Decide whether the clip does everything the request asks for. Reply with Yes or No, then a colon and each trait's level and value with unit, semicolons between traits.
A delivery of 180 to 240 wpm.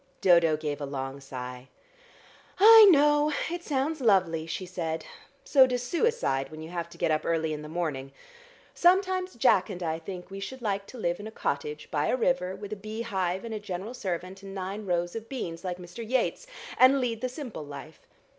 Yes: average, 200 wpm